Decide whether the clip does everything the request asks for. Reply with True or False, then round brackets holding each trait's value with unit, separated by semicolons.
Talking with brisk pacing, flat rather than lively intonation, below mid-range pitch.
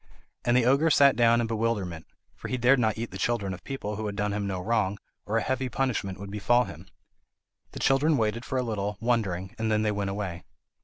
False (225 wpm; 3.4 semitones; 110 Hz)